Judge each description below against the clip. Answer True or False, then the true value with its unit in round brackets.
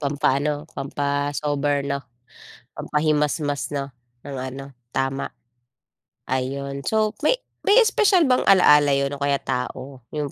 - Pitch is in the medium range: True (145 Hz)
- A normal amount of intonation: False (1.4 semitones)